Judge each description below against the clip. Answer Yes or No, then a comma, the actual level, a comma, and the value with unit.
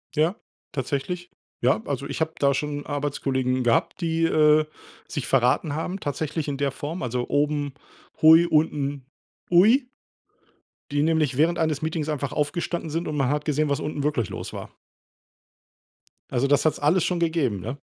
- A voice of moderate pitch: Yes, medium, 150 Hz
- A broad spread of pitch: No, narrow, 2.5 semitones